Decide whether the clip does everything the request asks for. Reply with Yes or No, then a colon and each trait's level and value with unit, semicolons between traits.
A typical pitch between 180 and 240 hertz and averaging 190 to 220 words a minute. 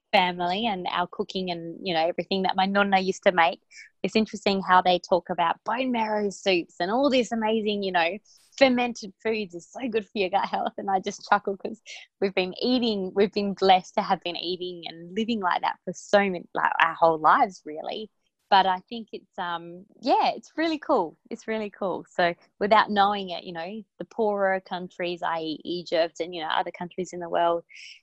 Yes: high, 190 Hz; fast, 205 wpm